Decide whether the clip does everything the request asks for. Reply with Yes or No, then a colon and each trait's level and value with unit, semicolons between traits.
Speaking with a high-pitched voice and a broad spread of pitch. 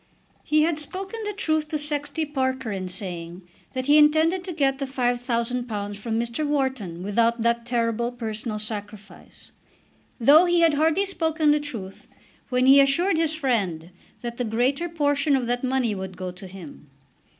Yes: very high, 255 Hz; wide, 5.7 semitones